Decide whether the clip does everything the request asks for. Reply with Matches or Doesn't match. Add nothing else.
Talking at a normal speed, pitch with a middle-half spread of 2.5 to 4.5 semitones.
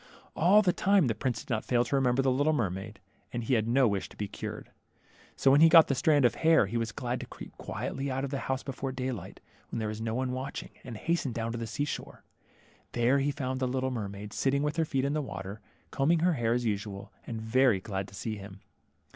Doesn't match